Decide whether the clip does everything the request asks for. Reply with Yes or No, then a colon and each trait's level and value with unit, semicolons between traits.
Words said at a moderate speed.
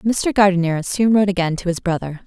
No: fast, 210 wpm